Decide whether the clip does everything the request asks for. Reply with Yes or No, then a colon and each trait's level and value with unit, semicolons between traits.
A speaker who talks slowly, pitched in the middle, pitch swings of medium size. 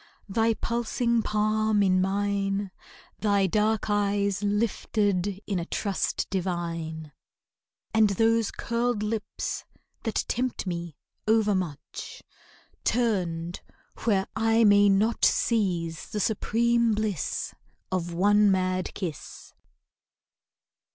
No: slow, 95 wpm; high, 205 Hz; average, 3.0 semitones